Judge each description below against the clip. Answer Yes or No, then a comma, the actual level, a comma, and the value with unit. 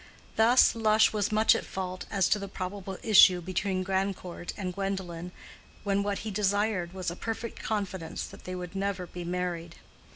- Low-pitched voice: No, high, 190 Hz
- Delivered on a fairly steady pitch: Yes, narrow, 2.1 semitones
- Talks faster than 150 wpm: Yes, average, 170 wpm